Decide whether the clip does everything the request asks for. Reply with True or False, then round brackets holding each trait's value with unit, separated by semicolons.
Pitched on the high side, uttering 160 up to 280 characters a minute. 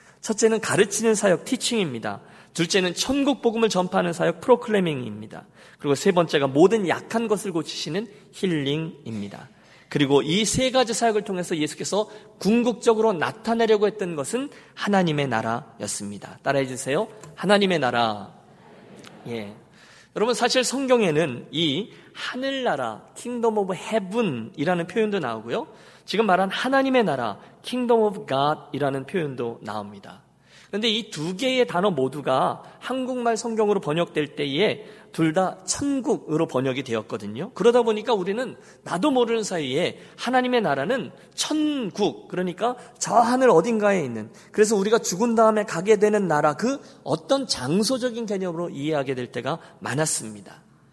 False (200 Hz; 345 characters per minute)